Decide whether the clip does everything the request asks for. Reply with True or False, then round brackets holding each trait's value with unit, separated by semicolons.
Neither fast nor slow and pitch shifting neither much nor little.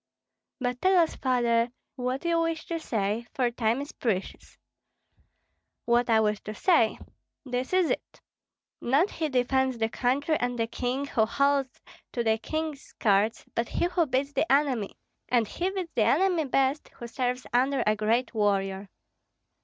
True (160 wpm; 3.9 semitones)